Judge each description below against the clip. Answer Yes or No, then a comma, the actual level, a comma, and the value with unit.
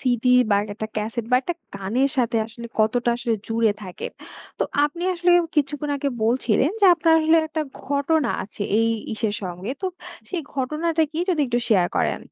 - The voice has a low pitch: No, very high, 250 Hz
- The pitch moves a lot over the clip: Yes, wide, 5.7 semitones